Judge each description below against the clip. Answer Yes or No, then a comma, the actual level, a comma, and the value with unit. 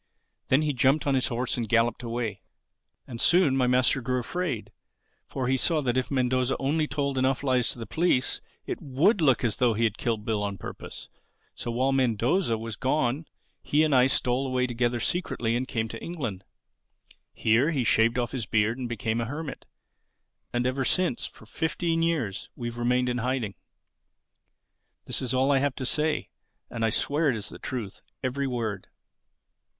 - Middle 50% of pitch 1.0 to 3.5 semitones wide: Yes, average, 2.9 semitones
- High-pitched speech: No, low, 125 Hz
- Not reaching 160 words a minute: No, average, 185 wpm